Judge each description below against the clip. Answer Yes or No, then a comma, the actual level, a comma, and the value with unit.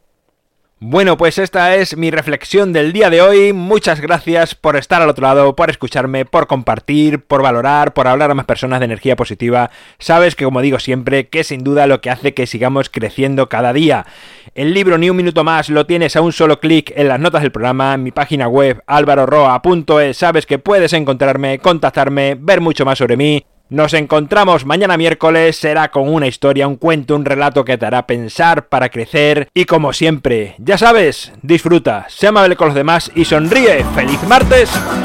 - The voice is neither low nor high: Yes, medium, 150 Hz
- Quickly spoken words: Yes, fast, 195 wpm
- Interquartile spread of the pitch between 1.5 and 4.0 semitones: Yes, average, 3.7 semitones